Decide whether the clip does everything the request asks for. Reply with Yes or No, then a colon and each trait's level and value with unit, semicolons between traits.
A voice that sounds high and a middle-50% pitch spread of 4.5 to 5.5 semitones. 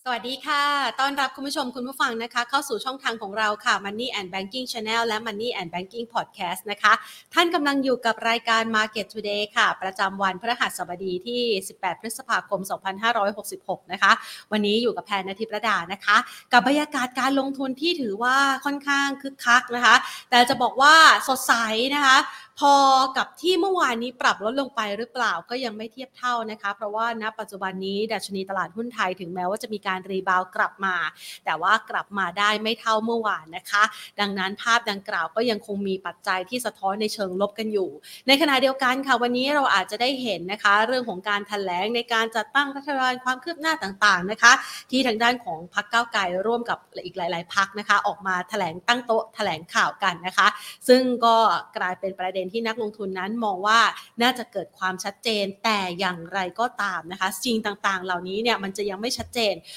No: high, 220 Hz; average, 4.1 semitones